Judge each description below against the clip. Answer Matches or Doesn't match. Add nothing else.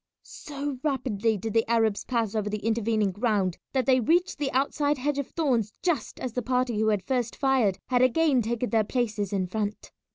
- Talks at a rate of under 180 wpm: Doesn't match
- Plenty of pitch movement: Doesn't match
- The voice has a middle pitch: Doesn't match